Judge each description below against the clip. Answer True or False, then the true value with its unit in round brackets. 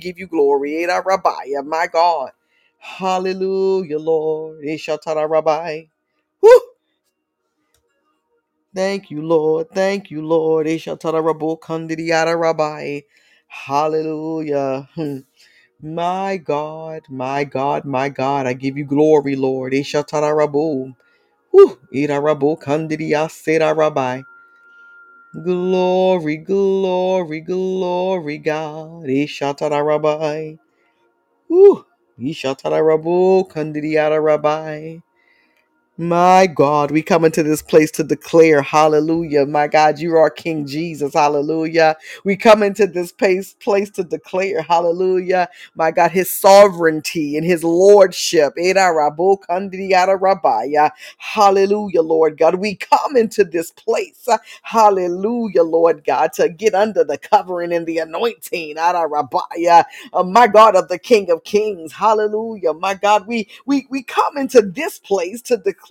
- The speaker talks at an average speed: False (115 wpm)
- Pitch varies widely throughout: False (4.0 semitones)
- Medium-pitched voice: True (165 Hz)